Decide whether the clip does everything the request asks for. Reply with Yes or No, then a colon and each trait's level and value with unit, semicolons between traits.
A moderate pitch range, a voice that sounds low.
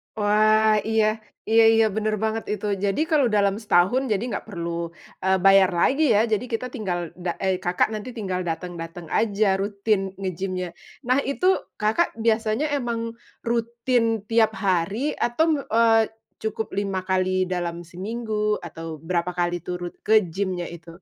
No: average, 3.7 semitones; high, 205 Hz